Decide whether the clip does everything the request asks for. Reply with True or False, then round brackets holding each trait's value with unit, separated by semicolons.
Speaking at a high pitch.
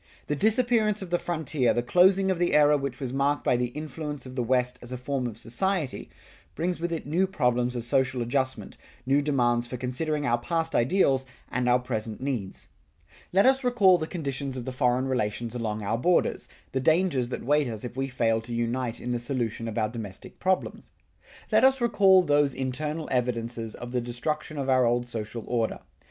False (130 Hz)